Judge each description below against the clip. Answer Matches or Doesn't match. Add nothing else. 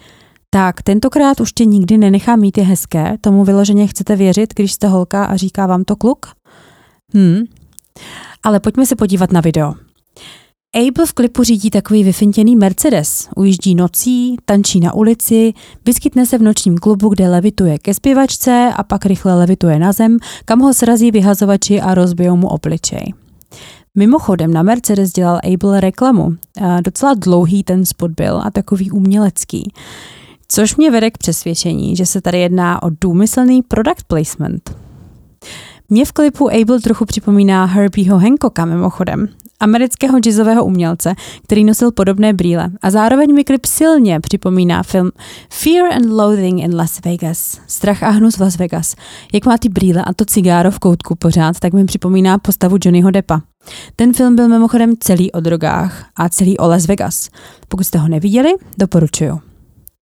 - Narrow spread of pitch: Doesn't match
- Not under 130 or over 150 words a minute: Doesn't match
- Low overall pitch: Doesn't match